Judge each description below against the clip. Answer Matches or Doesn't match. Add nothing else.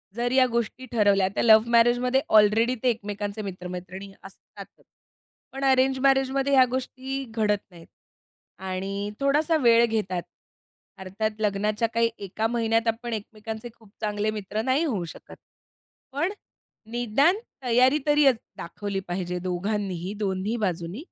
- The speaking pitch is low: Doesn't match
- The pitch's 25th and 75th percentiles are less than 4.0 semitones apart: Doesn't match